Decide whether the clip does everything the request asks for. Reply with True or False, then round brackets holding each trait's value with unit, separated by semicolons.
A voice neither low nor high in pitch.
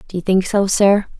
False (195 Hz)